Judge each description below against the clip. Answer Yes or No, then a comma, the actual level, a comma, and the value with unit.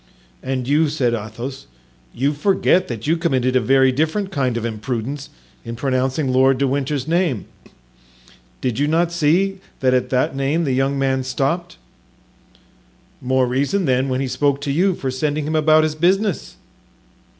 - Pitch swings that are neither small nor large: Yes, average, 3.4 semitones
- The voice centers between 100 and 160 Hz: Yes, low, 135 Hz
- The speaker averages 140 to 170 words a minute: Yes, average, 160 wpm